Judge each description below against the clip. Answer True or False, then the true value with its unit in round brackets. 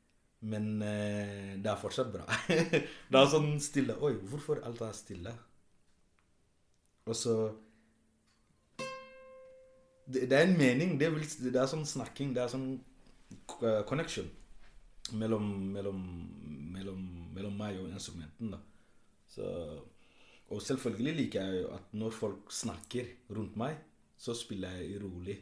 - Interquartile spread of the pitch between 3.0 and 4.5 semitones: False (5.1 semitones)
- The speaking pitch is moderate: False (110 Hz)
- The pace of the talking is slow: True (130 wpm)